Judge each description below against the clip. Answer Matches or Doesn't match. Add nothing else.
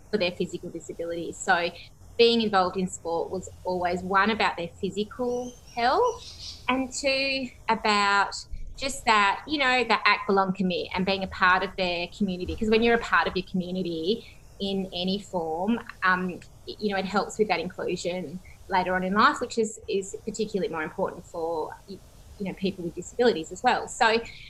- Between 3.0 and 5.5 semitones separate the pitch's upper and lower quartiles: Matches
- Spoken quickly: Doesn't match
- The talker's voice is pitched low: Doesn't match